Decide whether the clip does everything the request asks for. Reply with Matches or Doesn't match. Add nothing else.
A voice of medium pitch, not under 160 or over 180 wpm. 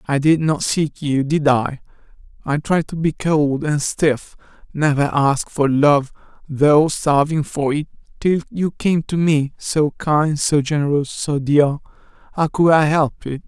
Matches